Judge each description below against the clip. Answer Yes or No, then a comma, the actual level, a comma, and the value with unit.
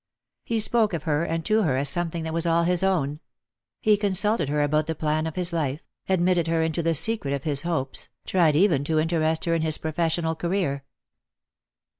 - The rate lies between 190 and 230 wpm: Yes, average, 200 wpm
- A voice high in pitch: No, medium, 165 Hz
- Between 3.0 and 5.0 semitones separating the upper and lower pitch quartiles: No, narrow, 2.5 semitones